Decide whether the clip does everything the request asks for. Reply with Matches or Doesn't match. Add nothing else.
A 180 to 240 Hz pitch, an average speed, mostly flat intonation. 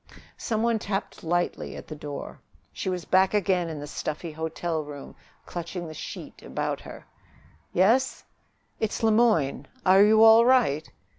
Doesn't match